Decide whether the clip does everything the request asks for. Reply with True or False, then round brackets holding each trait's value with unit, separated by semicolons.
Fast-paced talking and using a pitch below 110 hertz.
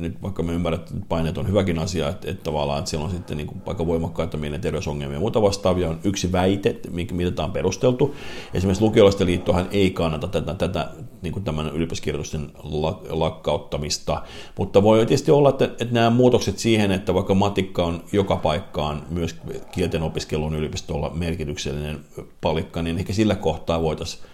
True (170 wpm; 85 Hz)